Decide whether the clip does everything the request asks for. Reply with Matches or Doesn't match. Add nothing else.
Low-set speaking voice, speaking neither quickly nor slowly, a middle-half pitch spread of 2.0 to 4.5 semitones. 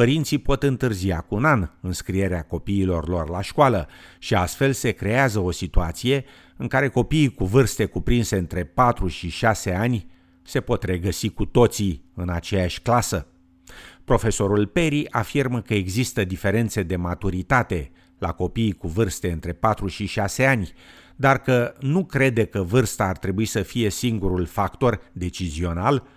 Doesn't match